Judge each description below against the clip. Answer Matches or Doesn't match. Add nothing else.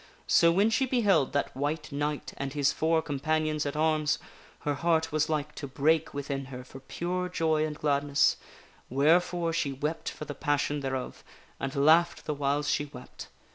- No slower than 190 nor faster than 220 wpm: Doesn't match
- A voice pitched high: Doesn't match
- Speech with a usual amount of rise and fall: Doesn't match